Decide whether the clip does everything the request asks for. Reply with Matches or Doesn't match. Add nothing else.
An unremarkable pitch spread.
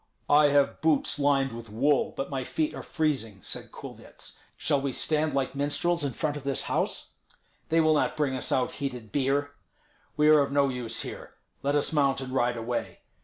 Doesn't match